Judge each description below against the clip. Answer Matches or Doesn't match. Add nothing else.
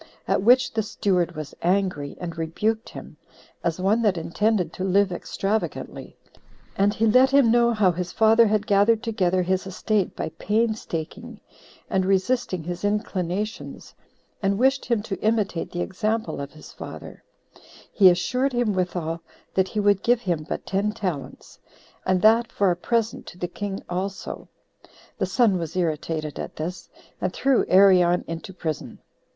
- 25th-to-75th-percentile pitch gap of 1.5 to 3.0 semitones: Doesn't match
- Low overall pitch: Doesn't match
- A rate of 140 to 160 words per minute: Matches